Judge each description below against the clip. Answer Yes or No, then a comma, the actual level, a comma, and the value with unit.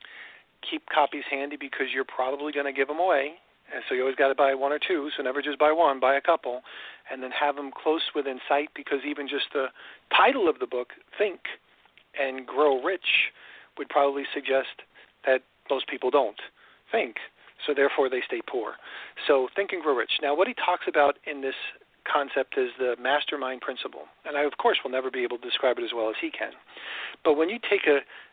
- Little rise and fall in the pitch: Yes, narrow, 2.2 semitones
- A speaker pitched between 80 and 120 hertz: No, medium, 140 Hz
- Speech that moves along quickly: Yes, fast, 210 wpm